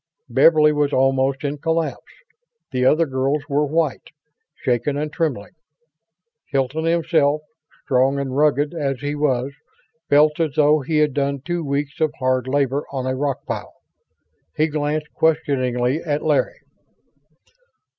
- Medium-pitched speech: Yes, medium, 145 Hz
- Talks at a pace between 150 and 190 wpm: No, slow, 135 wpm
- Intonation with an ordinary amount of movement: No, narrow, 2.3 semitones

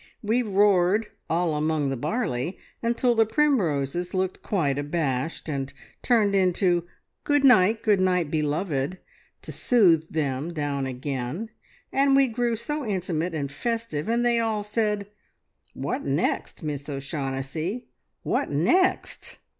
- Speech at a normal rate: No, slow, 130 wpm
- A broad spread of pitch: Yes, wide, 7.4 semitones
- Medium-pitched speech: Yes, medium, 180 Hz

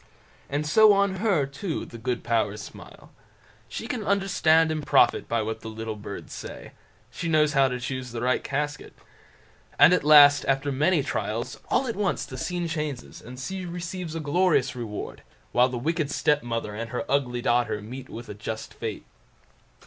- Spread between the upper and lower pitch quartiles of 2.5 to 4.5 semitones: No, wide, 5.5 semitones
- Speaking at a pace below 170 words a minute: No, average, 180 wpm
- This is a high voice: No, medium, 140 Hz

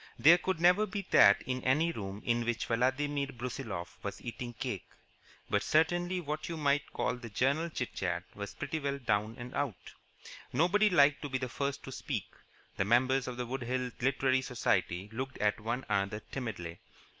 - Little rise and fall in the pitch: No, average, 4.0 semitones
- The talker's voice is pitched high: No, low, 130 Hz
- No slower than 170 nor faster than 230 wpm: Yes, average, 180 wpm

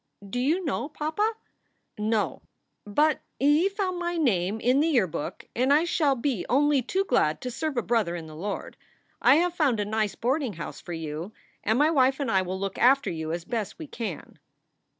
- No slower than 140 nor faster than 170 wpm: No, average, 195 wpm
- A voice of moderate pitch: No, very high, 250 Hz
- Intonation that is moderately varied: No, wide, 6.9 semitones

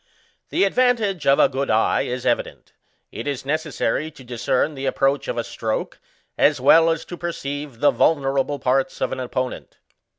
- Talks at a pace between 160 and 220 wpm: Yes, average, 170 wpm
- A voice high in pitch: No, medium, 140 Hz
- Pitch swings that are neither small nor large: Yes, average, 3.6 semitones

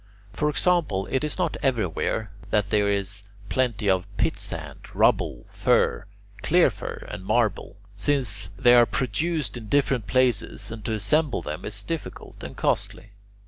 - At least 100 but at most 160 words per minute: Yes, average, 145 wpm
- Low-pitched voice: Yes, low, 110 Hz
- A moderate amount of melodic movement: Yes, average, 5.0 semitones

